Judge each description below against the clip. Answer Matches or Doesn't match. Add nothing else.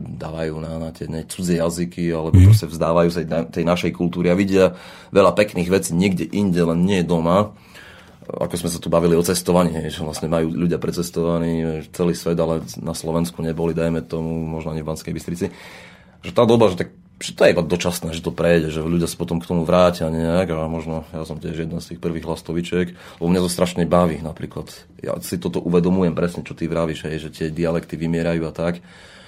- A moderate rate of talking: Doesn't match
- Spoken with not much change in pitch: Matches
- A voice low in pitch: Matches